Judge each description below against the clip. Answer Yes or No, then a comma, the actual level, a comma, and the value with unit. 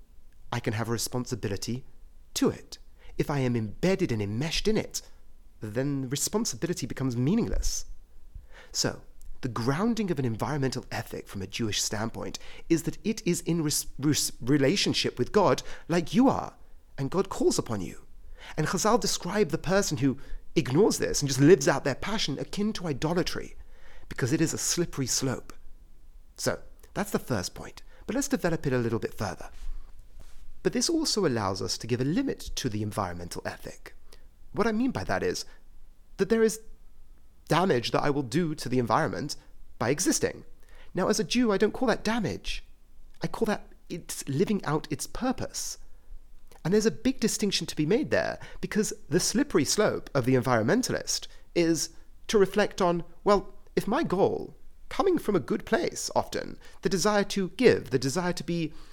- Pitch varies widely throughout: Yes, wide, 8.3 semitones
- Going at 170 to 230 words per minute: Yes, average, 175 wpm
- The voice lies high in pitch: No, medium, 155 Hz